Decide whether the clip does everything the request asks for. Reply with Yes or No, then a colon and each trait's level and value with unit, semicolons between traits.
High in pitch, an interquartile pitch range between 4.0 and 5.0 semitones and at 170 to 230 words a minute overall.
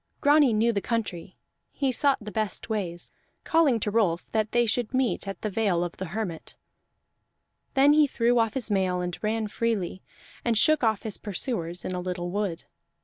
Yes: high, 215 Hz; average, 4.3 semitones; average, 185 wpm